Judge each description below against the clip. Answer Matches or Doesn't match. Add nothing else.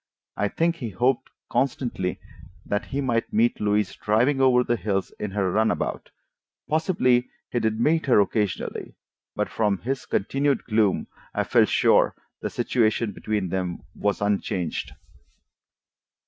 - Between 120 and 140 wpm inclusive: Matches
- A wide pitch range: Doesn't match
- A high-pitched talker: Doesn't match